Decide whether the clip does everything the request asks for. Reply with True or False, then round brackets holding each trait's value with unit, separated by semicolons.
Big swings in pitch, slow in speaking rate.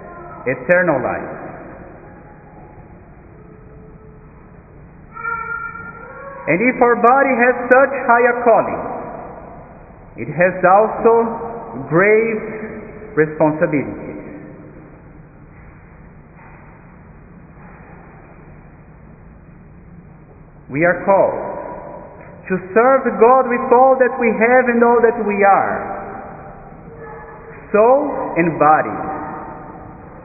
True (6.6 semitones; 65 wpm)